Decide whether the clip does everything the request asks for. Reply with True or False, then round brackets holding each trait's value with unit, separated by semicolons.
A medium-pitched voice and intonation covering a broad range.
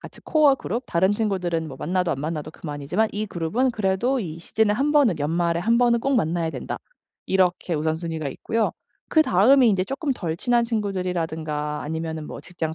True (180 Hz; 6.1 semitones)